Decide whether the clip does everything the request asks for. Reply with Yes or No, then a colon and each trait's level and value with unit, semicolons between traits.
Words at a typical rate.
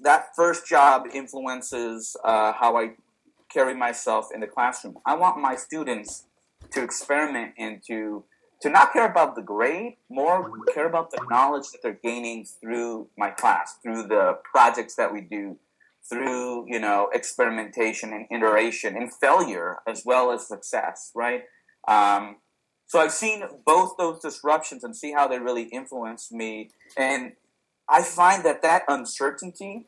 Yes: average, 155 wpm